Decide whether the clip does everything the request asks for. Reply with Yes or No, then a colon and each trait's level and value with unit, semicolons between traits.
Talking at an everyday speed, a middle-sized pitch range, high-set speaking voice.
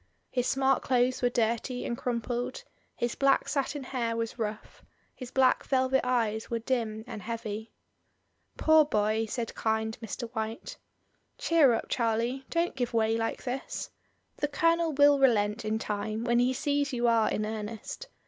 Yes: average, 160 wpm; average, 3.1 semitones; high, 240 Hz